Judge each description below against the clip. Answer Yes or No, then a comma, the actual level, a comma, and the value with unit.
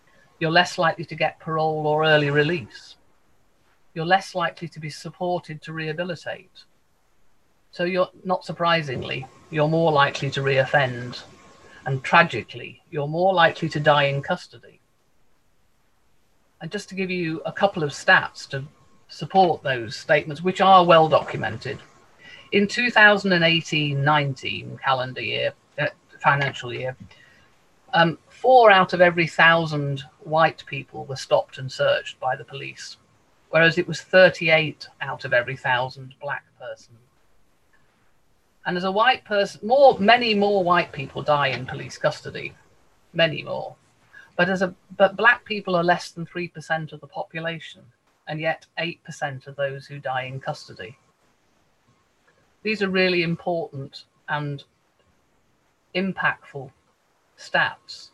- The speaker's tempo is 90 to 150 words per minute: Yes, slow, 135 wpm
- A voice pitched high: No, medium, 165 Hz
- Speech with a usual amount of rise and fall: Yes, average, 4.2 semitones